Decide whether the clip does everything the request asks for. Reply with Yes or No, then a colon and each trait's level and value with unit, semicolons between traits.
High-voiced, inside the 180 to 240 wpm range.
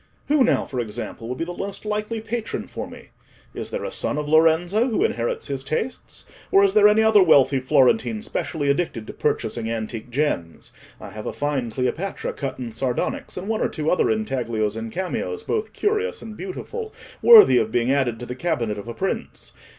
No: medium, 155 Hz; average, 195 wpm